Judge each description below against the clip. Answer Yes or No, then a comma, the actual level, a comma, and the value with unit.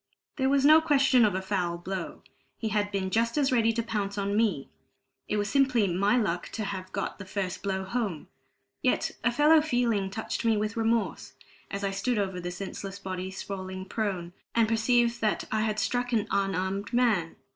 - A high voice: Yes, high, 205 Hz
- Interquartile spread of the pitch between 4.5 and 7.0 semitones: No, average, 3.6 semitones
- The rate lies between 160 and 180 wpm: No, average, 190 wpm